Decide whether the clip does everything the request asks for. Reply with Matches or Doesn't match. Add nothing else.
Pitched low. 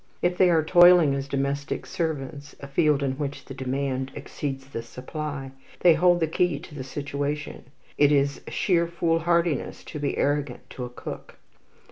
Doesn't match